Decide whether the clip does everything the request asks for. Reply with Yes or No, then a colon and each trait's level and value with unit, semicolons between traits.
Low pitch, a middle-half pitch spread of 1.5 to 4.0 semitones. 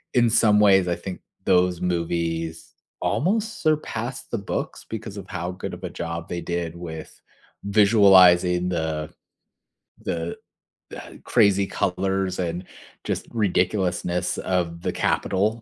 Yes: very low, 90 Hz; average, 2.9 semitones